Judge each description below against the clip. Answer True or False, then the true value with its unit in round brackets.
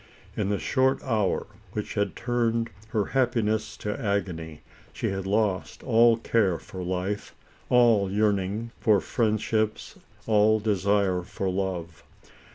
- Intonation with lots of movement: False (2.7 semitones)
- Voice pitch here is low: True (105 Hz)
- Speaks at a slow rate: True (130 wpm)